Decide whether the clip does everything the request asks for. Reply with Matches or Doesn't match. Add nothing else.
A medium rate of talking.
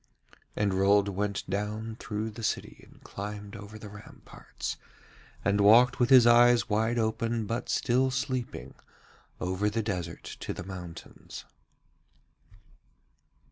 Doesn't match